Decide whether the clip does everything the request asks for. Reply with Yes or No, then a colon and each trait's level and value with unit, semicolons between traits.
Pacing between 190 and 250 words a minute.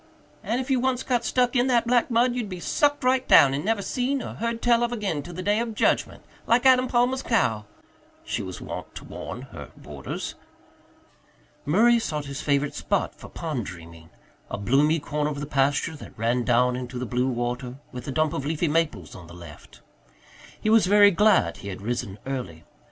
Yes: average, 200 wpm